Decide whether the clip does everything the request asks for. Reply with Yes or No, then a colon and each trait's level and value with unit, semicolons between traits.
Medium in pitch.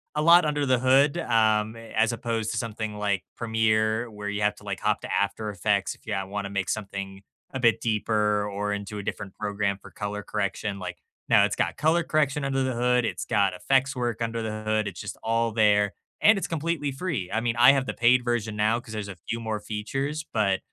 No: low, 110 Hz